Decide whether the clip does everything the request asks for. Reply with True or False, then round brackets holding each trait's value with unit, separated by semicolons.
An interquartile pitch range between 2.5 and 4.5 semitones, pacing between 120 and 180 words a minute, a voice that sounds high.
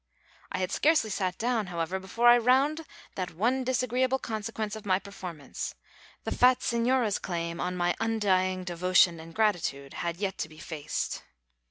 False (5.2 semitones; 160 wpm; 200 Hz)